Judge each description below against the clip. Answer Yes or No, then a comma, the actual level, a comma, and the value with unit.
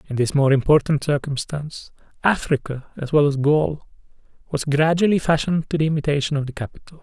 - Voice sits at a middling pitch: Yes, medium, 145 Hz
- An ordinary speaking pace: Yes, average, 160 wpm